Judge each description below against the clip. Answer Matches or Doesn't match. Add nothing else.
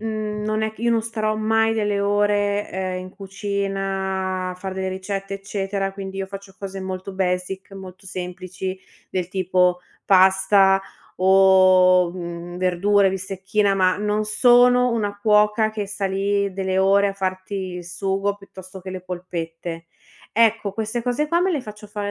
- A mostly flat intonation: Matches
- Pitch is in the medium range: Doesn't match